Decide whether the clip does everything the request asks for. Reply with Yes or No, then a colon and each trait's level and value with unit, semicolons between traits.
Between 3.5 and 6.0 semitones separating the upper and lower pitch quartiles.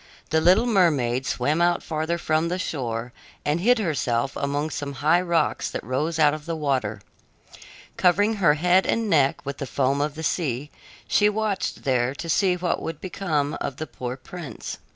Yes: average, 4.3 semitones